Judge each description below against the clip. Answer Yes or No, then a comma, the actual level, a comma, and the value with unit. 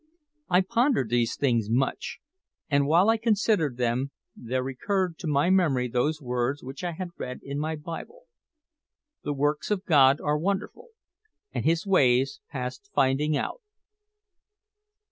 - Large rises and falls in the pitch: Yes, wide, 6.1 semitones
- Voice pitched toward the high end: No, medium, 145 Hz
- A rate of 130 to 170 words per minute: Yes, average, 145 wpm